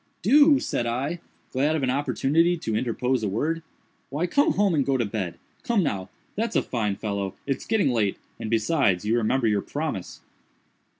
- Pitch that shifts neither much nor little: No, wide, 7.1 semitones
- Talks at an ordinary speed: Yes, average, 175 wpm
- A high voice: No, low, 130 Hz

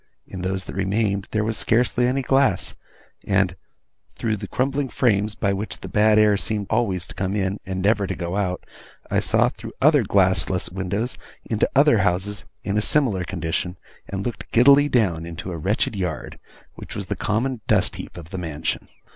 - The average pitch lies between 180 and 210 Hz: No, low, 100 Hz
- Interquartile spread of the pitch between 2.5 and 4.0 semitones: Yes, average, 3.4 semitones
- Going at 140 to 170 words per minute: No, average, 185 wpm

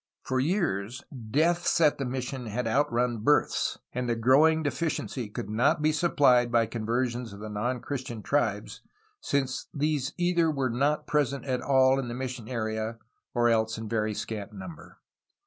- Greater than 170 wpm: No, average, 165 wpm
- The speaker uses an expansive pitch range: No, average, 4.1 semitones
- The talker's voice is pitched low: Yes, low, 125 Hz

